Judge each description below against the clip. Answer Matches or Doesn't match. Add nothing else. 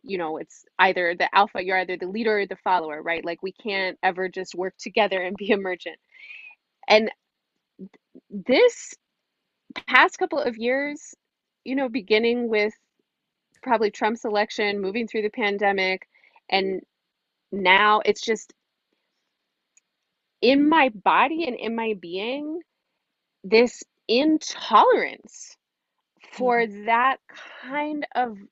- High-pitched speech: Matches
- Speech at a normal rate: Doesn't match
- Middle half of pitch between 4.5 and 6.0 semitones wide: Matches